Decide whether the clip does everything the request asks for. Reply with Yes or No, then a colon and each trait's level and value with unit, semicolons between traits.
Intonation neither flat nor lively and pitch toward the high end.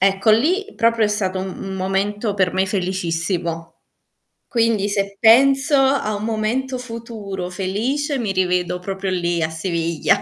Yes: average, 3.7 semitones; high, 200 Hz